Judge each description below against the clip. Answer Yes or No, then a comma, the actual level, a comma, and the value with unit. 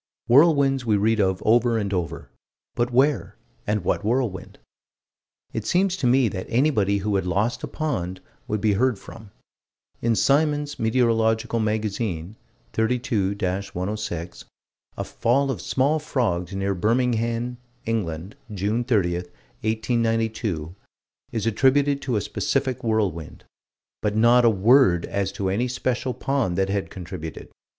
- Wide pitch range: No, average, 4.2 semitones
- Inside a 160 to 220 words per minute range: No, slow, 135 wpm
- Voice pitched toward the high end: No, low, 110 Hz